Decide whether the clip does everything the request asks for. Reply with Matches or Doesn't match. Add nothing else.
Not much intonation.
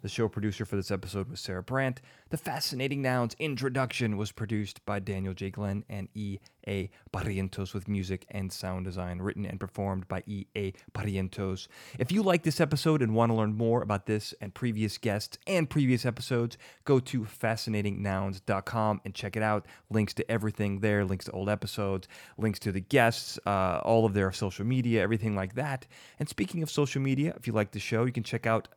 Doesn't match